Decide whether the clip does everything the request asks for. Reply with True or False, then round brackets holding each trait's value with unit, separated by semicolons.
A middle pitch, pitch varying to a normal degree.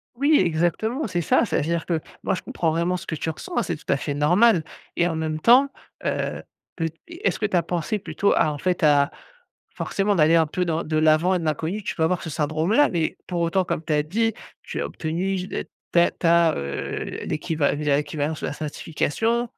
True (170 Hz; 3.5 semitones)